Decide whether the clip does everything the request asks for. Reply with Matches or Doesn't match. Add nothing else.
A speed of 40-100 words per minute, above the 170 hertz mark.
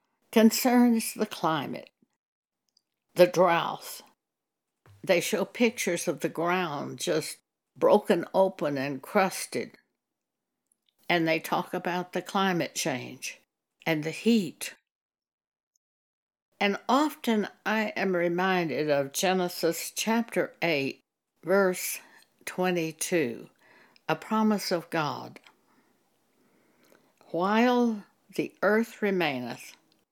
Matches